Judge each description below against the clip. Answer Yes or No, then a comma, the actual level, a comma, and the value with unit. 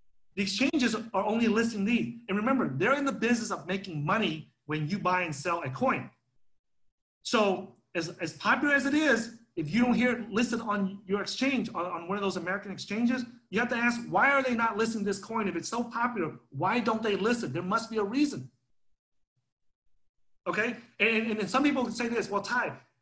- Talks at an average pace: No, fast, 210 wpm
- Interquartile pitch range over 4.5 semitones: Yes, wide, 5.6 semitones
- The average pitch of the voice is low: No, high, 210 Hz